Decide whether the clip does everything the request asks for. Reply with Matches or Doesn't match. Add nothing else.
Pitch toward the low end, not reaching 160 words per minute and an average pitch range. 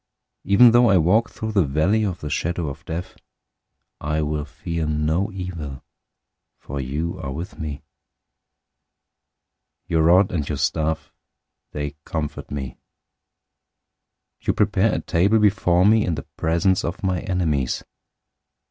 Matches